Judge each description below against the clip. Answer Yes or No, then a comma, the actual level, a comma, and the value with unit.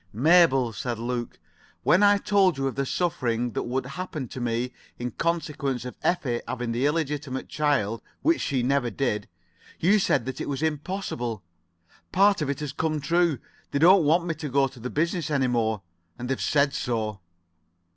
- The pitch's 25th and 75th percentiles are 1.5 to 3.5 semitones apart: No, average, 4.9 semitones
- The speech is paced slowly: No, average, 185 wpm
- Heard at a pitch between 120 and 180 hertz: Yes, medium, 140 Hz